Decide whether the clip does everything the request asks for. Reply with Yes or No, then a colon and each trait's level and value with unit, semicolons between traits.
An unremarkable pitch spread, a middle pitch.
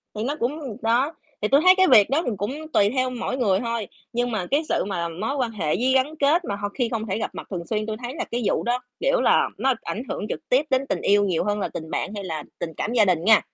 No: average, 4.5 semitones; high, 230 Hz